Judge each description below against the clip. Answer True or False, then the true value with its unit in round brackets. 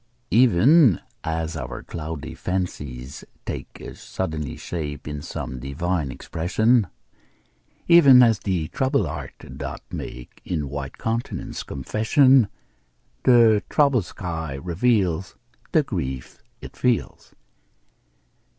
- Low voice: True (85 Hz)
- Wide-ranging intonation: True (8.0 semitones)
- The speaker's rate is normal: False (105 wpm)